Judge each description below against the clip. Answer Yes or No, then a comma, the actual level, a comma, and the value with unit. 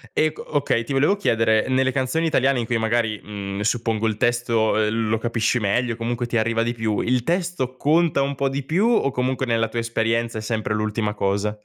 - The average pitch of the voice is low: Yes, low, 115 Hz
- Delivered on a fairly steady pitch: No, average, 3.0 semitones